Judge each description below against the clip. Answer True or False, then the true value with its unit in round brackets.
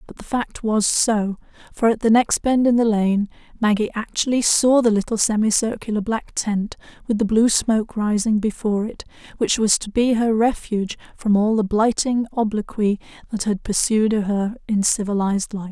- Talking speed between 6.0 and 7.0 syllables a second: False (5.0 syllables/s)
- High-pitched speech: True (215 Hz)